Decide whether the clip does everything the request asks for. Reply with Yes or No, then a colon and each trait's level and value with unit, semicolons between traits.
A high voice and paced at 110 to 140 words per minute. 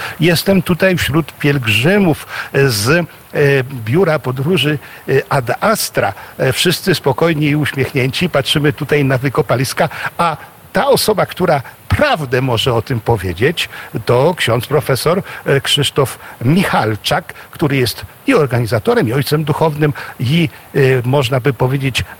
No: medium, 140 Hz; average, 115 wpm